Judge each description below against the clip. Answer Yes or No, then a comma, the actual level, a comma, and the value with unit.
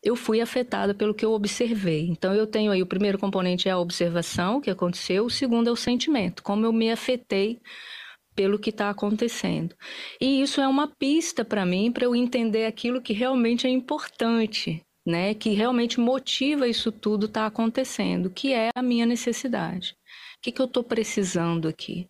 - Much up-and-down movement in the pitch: No, average, 3.7 semitones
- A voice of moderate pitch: No, high, 225 Hz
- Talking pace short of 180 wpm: No, fast, 185 wpm